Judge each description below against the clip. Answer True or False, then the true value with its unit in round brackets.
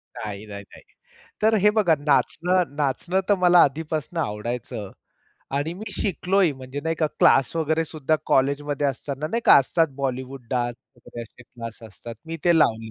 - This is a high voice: False (145 Hz)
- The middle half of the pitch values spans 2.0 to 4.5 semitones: False (5.0 semitones)